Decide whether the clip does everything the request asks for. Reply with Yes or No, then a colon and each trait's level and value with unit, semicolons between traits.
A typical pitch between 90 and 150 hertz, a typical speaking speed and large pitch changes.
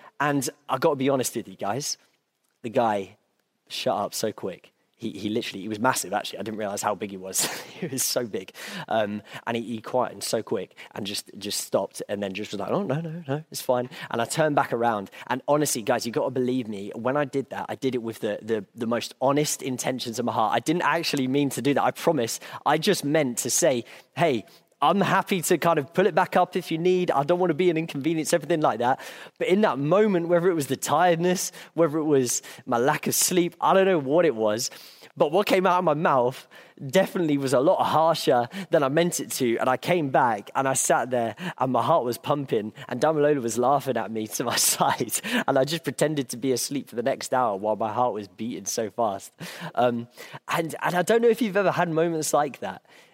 No: medium, 140 Hz; fast, 240 wpm; wide, 6.0 semitones